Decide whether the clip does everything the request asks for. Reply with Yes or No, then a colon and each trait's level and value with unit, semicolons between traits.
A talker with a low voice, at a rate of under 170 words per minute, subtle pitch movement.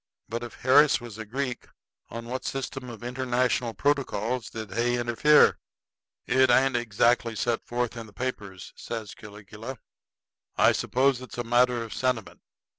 Yes: low, 120 Hz; average, 150 wpm; narrow, 2.2 semitones